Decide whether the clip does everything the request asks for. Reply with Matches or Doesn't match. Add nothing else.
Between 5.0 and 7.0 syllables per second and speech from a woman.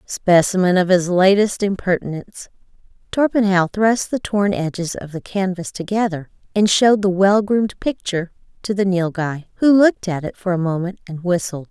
Matches